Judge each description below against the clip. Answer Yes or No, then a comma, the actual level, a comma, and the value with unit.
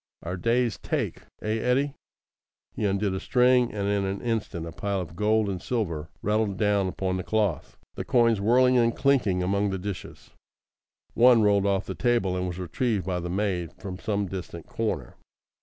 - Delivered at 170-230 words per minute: Yes, average, 180 wpm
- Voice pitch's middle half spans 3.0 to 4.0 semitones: Yes, average, 3.7 semitones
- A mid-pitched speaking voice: No, low, 100 Hz